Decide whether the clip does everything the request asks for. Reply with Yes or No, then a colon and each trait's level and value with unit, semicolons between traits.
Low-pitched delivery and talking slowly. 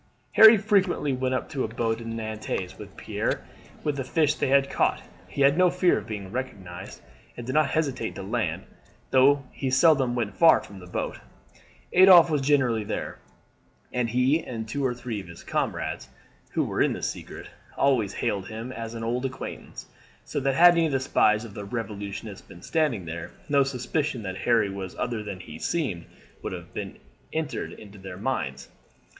No: low, 125 Hz; average, 185 wpm